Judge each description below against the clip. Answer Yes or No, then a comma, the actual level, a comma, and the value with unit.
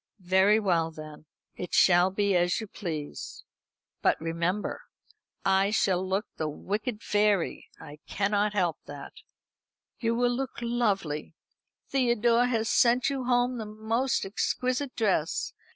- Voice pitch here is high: Yes, high, 205 Hz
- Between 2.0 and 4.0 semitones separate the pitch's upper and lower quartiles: No, average, 5.1 semitones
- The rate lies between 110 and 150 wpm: Yes, slow, 135 wpm